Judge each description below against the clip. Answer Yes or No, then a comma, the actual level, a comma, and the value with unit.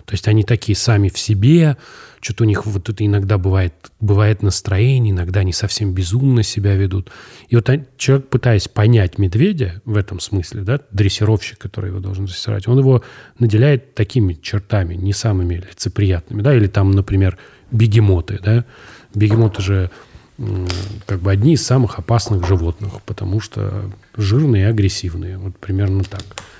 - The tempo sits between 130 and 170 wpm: Yes, average, 155 wpm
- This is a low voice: Yes, low, 105 Hz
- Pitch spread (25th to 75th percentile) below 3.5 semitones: Yes, average, 2.8 semitones